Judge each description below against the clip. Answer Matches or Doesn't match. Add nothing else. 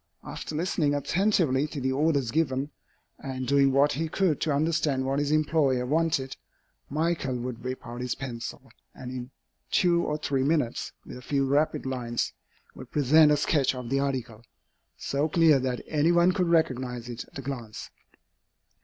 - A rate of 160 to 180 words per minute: Matches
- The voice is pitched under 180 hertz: Matches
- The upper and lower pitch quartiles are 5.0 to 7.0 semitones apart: Doesn't match